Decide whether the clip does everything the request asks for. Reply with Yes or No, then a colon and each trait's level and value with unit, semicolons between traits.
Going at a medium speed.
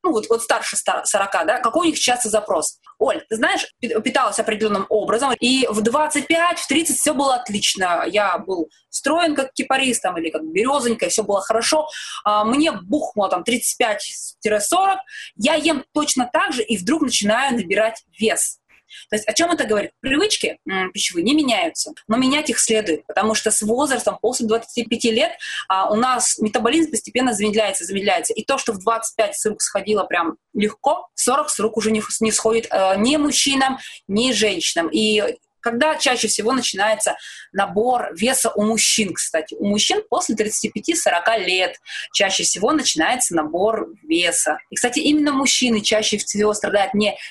No: fast, 165 wpm